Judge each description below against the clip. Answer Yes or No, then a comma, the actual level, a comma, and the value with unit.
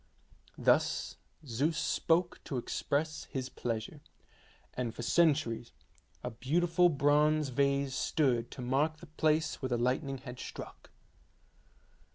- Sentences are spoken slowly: Yes, slow, 120 wpm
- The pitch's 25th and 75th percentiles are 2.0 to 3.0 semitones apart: No, average, 3.9 semitones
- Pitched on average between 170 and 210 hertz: No, medium, 140 Hz